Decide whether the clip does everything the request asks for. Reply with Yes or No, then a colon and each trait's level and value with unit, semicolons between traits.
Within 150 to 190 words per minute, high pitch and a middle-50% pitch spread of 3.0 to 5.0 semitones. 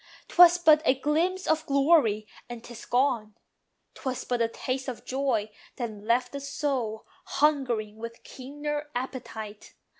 No: average, 140 wpm; very high, 260 Hz; average, 4.3 semitones